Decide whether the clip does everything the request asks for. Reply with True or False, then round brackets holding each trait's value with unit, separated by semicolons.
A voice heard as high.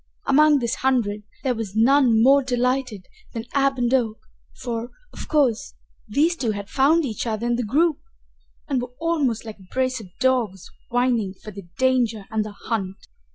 True (245 Hz)